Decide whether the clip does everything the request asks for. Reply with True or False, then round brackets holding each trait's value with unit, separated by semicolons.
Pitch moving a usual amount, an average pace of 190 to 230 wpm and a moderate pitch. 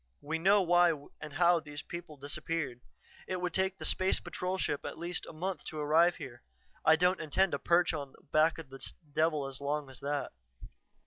True (3.5 semitones; 200 wpm; 160 Hz)